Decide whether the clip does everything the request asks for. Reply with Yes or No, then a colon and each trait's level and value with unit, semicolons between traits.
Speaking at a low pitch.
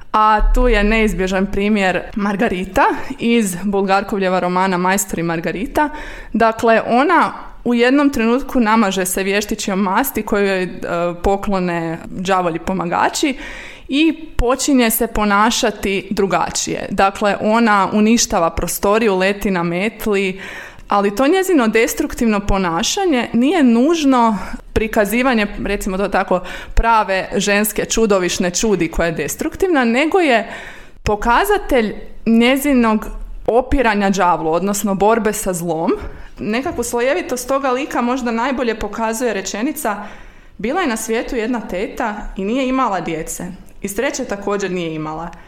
No: high, 215 Hz